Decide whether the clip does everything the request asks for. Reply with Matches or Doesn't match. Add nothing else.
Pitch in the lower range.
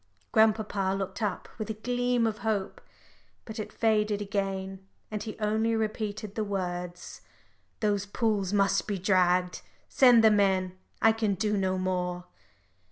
Doesn't match